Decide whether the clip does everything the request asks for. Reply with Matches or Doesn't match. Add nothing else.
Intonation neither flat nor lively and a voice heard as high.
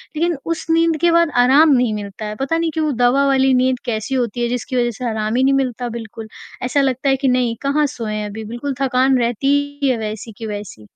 Matches